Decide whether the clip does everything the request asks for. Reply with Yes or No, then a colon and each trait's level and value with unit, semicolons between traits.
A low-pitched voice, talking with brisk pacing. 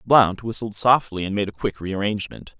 Yes: low, 105 Hz; fast, 210 wpm